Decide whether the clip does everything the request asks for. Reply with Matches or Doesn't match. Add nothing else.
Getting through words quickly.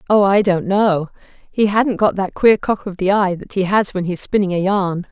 Matches